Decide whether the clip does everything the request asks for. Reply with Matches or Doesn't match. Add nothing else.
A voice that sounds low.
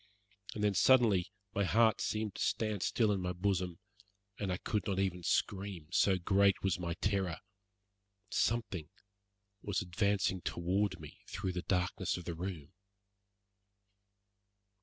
Matches